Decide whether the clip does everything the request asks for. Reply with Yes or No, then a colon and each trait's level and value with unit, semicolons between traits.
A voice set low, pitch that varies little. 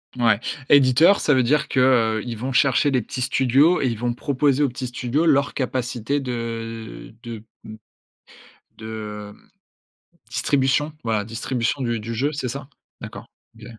No: low, 125 Hz; average, 3.2 semitones